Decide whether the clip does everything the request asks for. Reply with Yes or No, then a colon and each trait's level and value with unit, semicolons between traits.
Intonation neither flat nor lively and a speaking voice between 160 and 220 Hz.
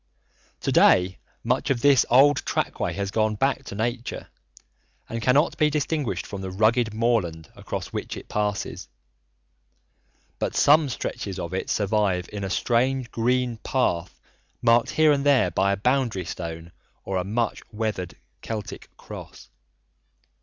No: average, 4.9 semitones; low, 110 Hz